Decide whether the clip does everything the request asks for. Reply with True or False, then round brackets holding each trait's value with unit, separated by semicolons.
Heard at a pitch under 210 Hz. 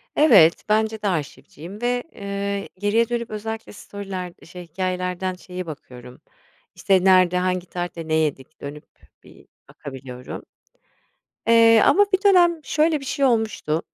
True (190 Hz)